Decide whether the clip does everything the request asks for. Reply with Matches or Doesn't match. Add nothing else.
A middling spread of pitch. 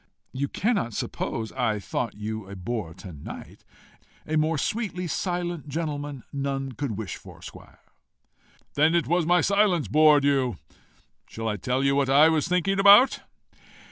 Doesn't match